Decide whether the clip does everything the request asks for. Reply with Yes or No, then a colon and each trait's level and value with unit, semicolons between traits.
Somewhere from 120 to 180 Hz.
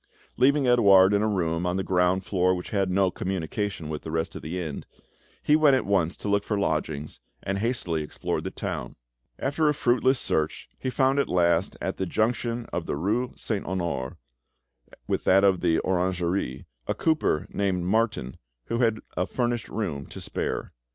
No: very low, 95 Hz